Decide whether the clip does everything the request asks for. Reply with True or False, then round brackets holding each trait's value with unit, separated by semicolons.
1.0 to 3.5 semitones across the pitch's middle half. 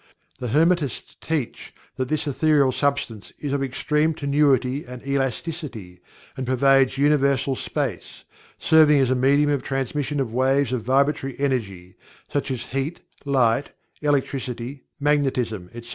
True (2.4 semitones)